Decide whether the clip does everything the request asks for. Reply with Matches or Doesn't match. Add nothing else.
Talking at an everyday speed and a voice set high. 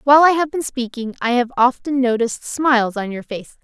Doesn't match